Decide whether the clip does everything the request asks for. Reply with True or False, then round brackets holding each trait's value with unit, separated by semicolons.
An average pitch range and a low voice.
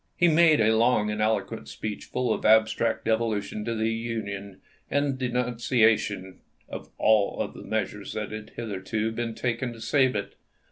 False (2.0 semitones; 110 Hz)